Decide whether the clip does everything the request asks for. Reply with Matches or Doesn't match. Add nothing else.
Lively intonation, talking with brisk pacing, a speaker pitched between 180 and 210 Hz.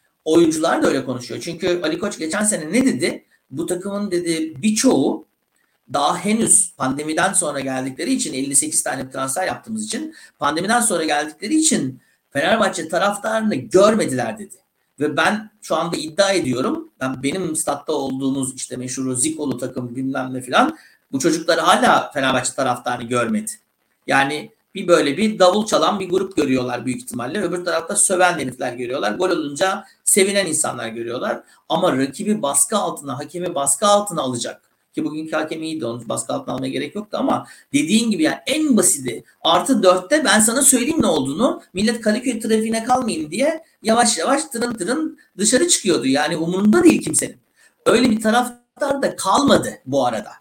Matches